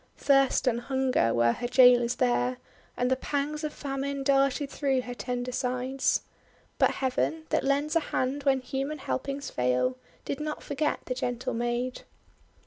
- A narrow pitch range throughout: Yes, narrow, 2.2 semitones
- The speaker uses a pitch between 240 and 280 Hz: Yes, very high, 260 Hz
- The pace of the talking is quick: No, average, 155 wpm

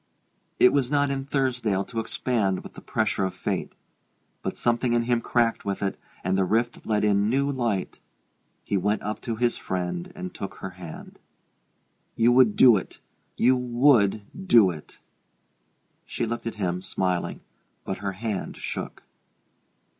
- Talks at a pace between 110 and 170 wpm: Yes, average, 160 wpm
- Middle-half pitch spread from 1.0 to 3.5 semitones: No, average, 4.1 semitones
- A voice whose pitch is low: Yes, low, 115 Hz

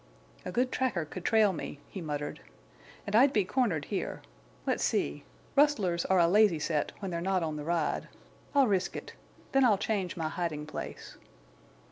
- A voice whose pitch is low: No, medium, 185 Hz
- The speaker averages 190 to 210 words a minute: No, average, 175 wpm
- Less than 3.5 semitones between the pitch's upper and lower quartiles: No, average, 4.9 semitones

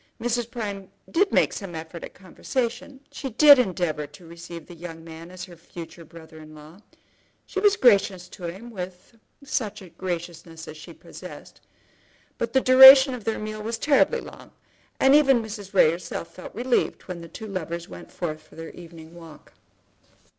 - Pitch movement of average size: No, wide, 5.9 semitones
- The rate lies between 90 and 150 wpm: No, average, 175 wpm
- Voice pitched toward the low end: No, medium, 185 Hz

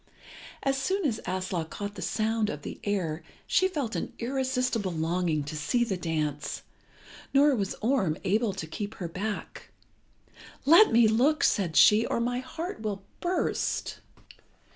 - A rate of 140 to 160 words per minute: Yes, average, 150 wpm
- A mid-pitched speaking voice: No, high, 215 Hz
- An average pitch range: No, wide, 5.9 semitones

